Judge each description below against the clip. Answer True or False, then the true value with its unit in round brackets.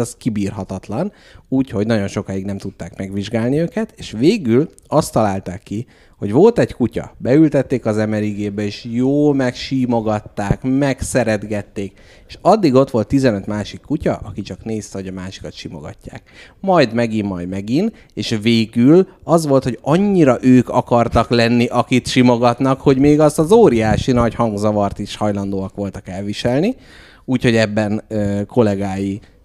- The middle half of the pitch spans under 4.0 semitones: False (4.3 semitones)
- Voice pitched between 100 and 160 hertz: True (110 Hz)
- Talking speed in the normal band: True (140 wpm)